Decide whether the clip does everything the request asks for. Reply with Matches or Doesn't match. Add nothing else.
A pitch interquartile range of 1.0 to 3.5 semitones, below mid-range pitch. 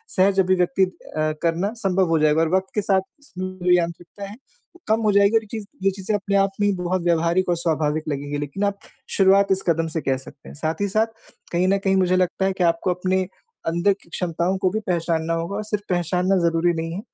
Doesn't match